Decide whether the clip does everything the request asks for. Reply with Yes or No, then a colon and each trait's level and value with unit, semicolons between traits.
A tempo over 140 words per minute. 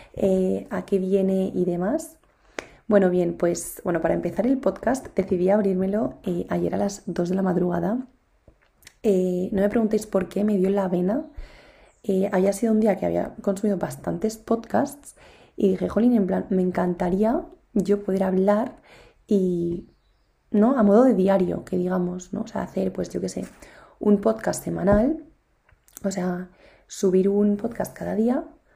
Yes: average, 165 wpm